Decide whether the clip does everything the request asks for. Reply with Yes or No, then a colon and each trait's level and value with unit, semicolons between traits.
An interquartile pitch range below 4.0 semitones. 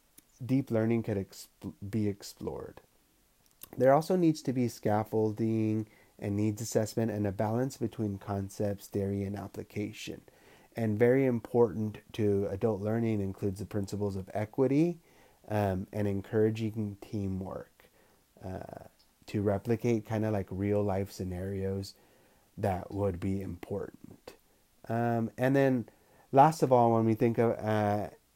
Yes: narrow, 2.4 semitones